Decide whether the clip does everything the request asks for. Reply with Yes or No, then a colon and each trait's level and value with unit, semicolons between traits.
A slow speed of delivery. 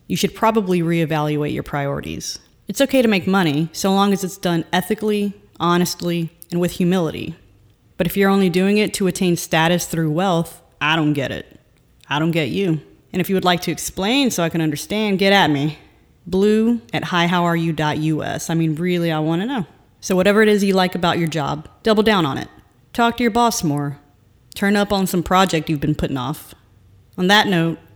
No: average, 200 wpm